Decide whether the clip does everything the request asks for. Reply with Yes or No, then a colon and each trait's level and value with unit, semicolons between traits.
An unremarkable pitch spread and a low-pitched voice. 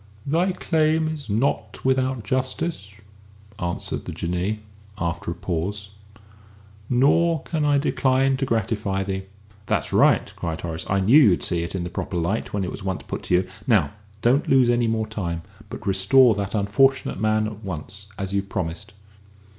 No: wide, 5.9 semitones; low, 105 Hz